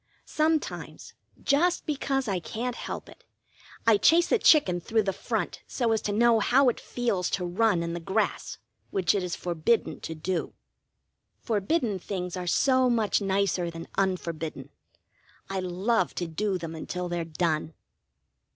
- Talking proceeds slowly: No, average, 155 wpm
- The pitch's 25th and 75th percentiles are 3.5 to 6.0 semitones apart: Yes, average, 5.1 semitones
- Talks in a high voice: Yes, high, 195 Hz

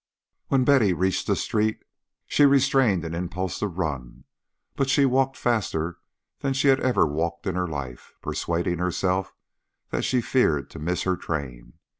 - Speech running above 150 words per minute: Yes, average, 160 wpm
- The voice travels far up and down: Yes, wide, 7.6 semitones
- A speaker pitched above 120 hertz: No, very low, 95 Hz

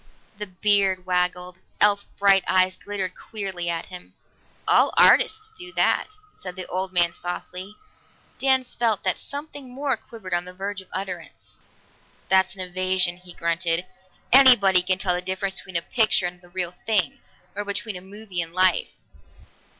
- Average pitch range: No, narrow, 2.3 semitones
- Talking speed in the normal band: Yes, average, 160 wpm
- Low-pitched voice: No, medium, 185 Hz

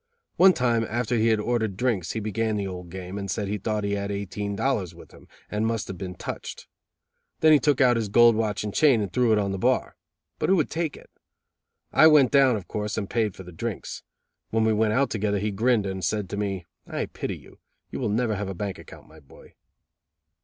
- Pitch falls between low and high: No, low, 105 Hz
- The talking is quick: Yes, fast, 230 wpm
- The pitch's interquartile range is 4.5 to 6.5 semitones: No, average, 3.2 semitones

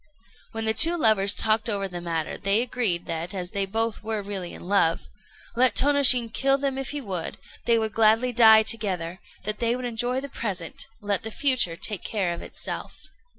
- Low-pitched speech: No, high, 220 Hz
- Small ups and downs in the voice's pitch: No, average, 4.0 semitones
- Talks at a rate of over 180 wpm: Yes, average, 190 wpm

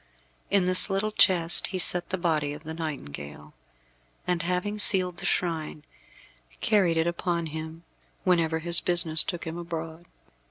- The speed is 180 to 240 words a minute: No, average, 150 wpm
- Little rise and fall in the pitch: Yes, narrow, 2.1 semitones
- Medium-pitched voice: Yes, medium, 170 Hz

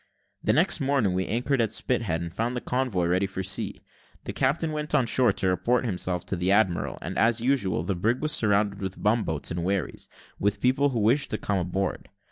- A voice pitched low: Yes, low, 105 Hz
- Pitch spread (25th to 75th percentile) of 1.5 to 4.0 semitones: No, average, 5.1 semitones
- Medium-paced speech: No, fast, 220 wpm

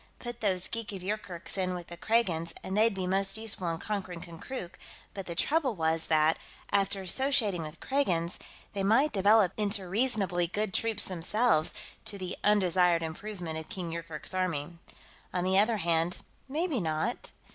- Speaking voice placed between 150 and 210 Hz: Yes, high, 190 Hz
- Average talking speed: Yes, average, 165 wpm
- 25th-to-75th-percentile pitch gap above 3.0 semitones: Yes, average, 4.0 semitones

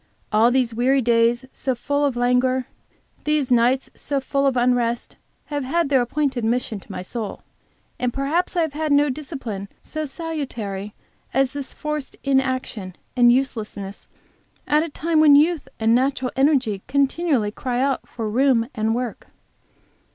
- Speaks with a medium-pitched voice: No, very high, 260 Hz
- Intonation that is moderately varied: Yes, average, 3.4 semitones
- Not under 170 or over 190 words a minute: No, average, 155 wpm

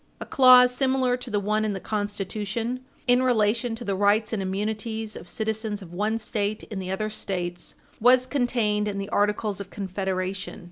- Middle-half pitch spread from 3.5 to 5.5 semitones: No, average, 2.8 semitones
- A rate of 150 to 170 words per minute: No, average, 180 wpm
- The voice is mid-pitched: No, high, 215 Hz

